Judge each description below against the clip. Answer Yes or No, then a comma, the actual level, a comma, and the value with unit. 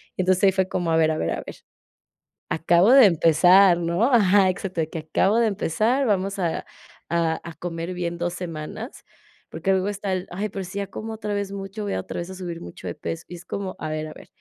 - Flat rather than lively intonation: No, average, 3.0 semitones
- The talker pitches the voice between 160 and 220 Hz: Yes, medium, 185 Hz